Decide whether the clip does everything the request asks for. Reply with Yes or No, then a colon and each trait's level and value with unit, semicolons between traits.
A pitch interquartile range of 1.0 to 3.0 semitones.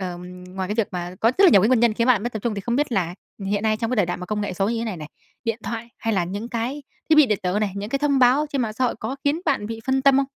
No: average, 4.3 semitones